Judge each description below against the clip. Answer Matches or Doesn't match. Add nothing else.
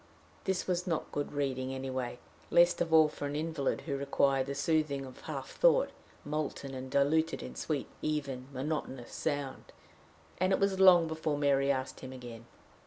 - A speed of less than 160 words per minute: Doesn't match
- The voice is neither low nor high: Matches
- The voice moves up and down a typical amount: Matches